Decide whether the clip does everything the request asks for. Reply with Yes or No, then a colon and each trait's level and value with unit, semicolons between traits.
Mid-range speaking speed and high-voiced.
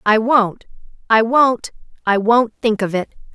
Yes: average, 160 wpm; high, 225 Hz